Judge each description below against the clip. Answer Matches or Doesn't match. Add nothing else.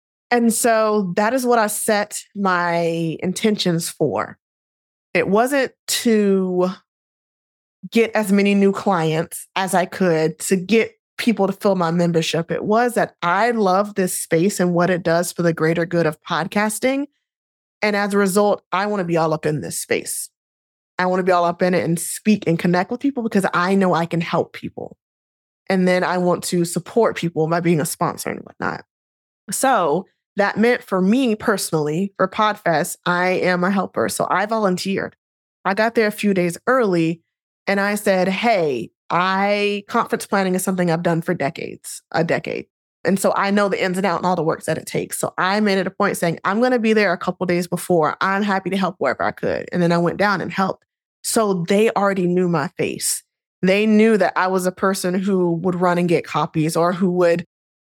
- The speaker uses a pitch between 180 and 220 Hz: Matches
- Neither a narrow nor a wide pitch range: Matches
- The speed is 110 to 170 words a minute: Doesn't match